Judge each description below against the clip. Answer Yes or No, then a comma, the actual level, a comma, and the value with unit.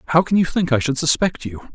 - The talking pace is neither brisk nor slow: No, fast, 275 wpm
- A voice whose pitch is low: No, medium, 150 Hz